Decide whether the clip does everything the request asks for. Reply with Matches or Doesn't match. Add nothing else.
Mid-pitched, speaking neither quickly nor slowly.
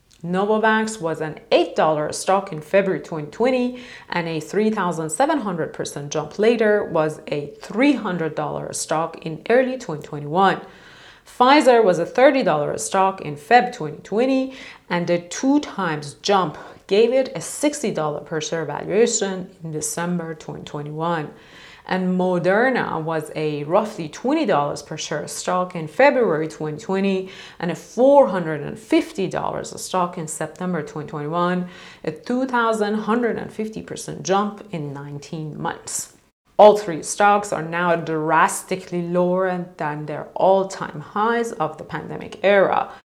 Doesn't match